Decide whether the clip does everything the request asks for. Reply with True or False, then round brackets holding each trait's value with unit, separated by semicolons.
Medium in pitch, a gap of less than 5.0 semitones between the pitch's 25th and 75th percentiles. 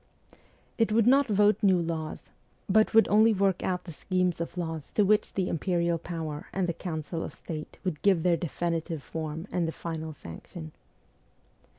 True (175 Hz; 3.3 semitones)